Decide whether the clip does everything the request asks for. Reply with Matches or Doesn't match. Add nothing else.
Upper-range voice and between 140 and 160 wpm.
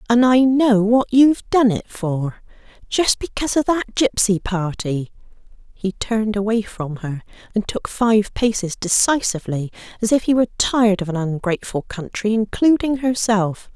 Matches